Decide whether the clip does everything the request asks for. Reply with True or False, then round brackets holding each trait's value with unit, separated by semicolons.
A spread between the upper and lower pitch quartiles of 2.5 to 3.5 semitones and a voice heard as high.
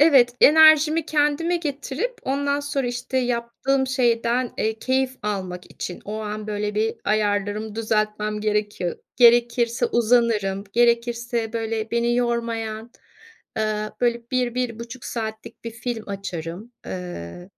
True (2.9 semitones; 235 Hz)